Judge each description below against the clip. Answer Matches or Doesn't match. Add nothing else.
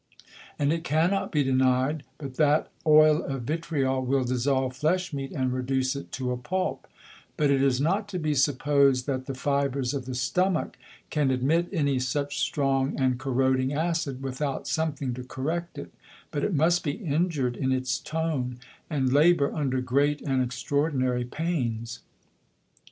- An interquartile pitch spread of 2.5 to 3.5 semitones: Matches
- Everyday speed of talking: Matches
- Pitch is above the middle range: Doesn't match